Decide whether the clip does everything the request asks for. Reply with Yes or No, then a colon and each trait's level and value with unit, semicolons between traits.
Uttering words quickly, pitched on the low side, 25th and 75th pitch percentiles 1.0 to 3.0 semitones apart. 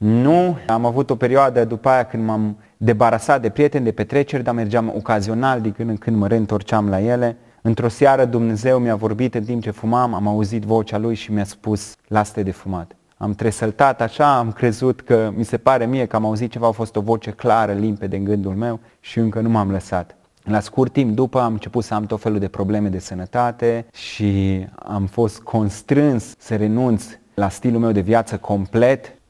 Yes: fast, 205 wpm; low, 115 Hz; narrow, 2.4 semitones